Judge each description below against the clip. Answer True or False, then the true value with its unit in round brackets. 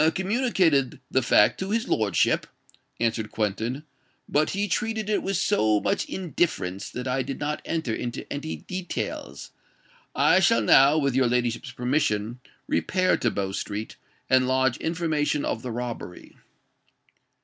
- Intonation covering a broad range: True (6.8 semitones)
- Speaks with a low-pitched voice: True (130 Hz)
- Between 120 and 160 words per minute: True (145 wpm)